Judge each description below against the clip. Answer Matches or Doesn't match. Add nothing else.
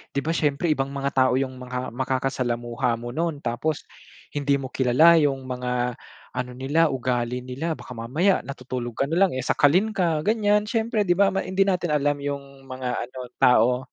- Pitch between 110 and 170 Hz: Matches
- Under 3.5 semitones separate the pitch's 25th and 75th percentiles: Doesn't match